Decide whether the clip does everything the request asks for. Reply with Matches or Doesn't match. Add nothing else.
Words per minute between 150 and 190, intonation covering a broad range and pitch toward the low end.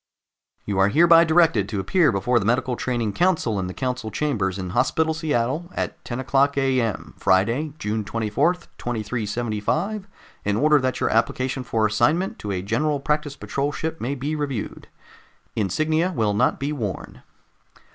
Matches